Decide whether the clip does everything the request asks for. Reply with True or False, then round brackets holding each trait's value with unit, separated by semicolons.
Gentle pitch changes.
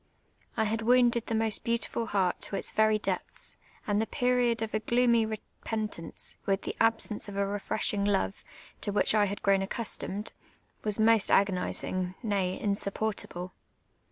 True (2.2 semitones)